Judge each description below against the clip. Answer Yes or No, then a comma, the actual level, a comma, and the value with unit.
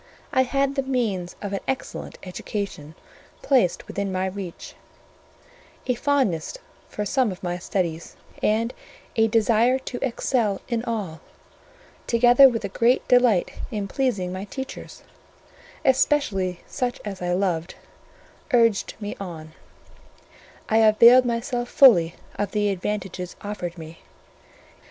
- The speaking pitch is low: No, high, 210 Hz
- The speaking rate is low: Yes, slow, 125 wpm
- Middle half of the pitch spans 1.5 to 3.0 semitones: No, average, 4.9 semitones